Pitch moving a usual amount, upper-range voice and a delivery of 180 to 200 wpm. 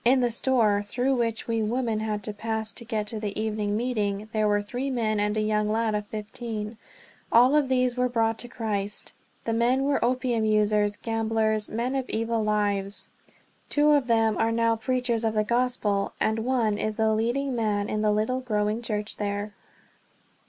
No: narrow, 2.2 semitones; high, 220 Hz; average, 190 wpm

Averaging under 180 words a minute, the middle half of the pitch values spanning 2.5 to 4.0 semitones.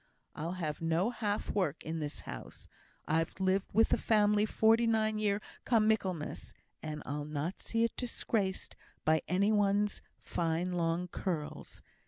No: average, 150 wpm; average, 4.7 semitones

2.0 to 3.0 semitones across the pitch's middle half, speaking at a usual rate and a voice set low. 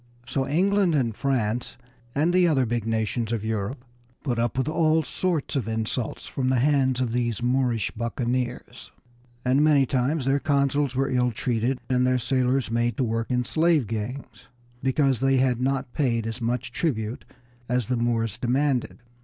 Yes: average, 2.7 semitones; average, 170 wpm; low, 125 Hz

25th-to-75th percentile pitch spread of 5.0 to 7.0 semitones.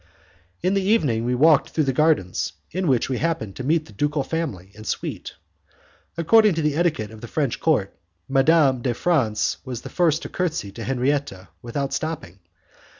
Yes: wide, 5.6 semitones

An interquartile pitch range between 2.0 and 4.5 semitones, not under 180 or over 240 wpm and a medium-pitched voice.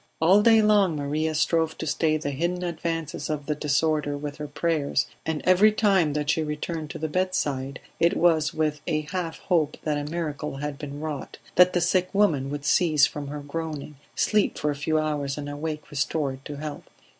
Yes: narrow, 2.4 semitones; average, 195 wpm; medium, 155 Hz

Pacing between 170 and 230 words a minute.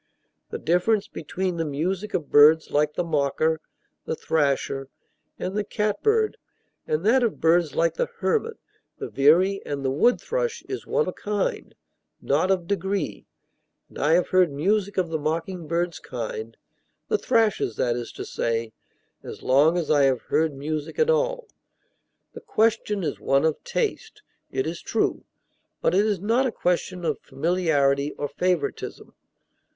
No: average, 160 wpm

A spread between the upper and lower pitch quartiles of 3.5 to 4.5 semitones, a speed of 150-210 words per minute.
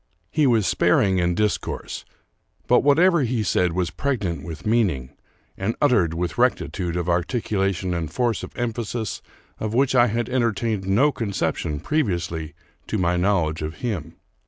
No: wide, 5.5 semitones; average, 155 wpm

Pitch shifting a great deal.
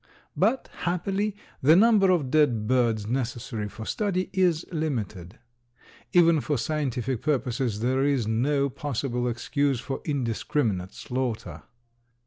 No: average, 5.0 semitones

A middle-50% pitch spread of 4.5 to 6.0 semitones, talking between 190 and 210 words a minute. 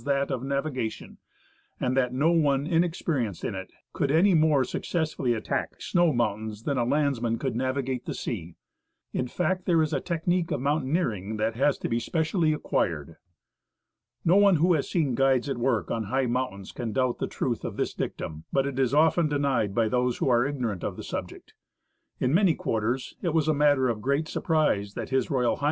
Yes: average, 4.8 semitones; average, 195 wpm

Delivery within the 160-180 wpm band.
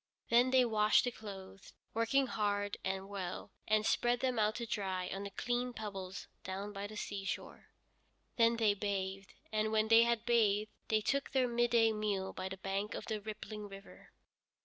Yes: average, 175 wpm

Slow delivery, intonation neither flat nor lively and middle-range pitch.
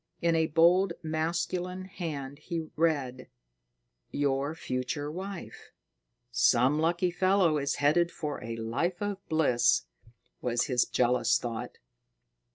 Yes: slow, 115 wpm; average, 4.5 semitones; medium, 155 Hz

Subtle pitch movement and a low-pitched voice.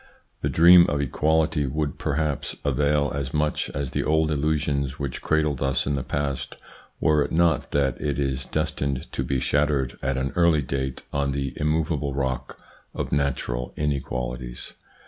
Yes: narrow, 2.2 semitones; very low, 70 Hz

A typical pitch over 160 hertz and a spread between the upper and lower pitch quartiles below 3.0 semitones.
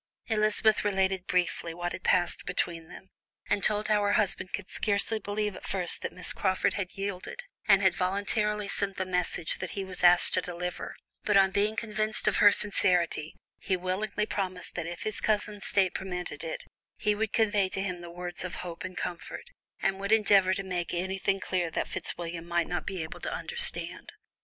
Yes: high, 190 Hz; narrow, 2.6 semitones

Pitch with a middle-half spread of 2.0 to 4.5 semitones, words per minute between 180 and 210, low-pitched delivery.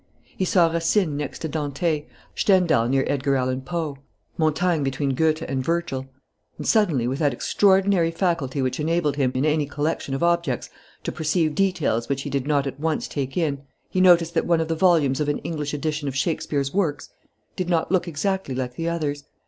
No: average, 3.6 semitones; average, 190 wpm; medium, 155 Hz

